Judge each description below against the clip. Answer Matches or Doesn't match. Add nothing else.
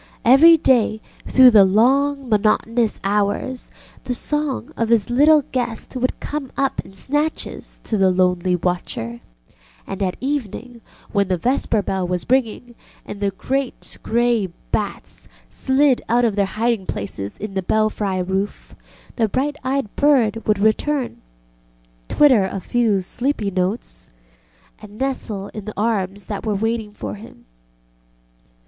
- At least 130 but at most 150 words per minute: Matches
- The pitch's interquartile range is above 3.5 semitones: Matches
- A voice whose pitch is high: Matches